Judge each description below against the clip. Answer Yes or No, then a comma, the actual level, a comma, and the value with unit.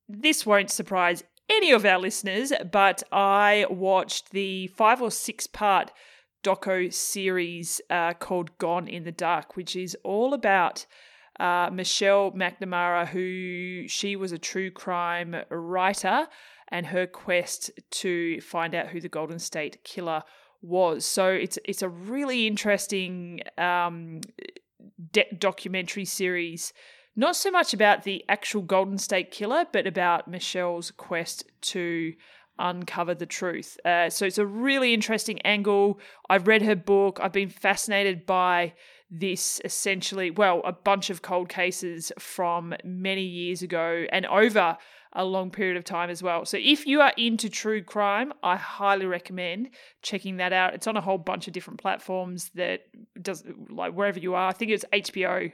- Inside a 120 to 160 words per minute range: Yes, average, 155 wpm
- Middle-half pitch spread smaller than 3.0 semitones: Yes, narrow, 2.5 semitones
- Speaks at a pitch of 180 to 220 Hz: Yes, high, 190 Hz